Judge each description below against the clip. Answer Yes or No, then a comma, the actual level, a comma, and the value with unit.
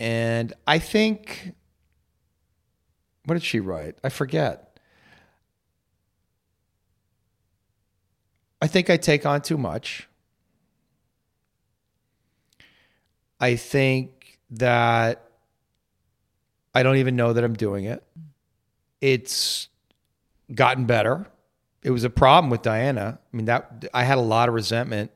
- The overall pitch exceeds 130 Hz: No, low, 115 Hz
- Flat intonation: No, average, 4.3 semitones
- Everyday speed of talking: No, slow, 105 wpm